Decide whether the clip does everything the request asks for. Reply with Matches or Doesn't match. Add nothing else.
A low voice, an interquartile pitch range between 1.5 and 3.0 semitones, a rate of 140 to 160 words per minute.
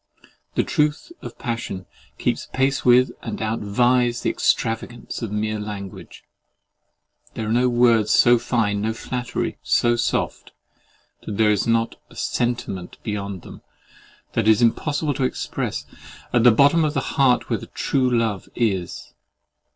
Matches